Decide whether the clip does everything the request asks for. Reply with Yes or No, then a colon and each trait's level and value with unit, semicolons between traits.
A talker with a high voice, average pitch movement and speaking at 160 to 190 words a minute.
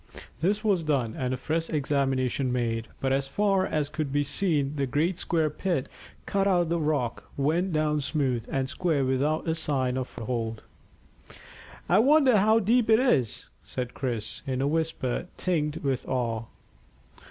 No: medium, 145 Hz; average, 4.8 semitones; average, 165 wpm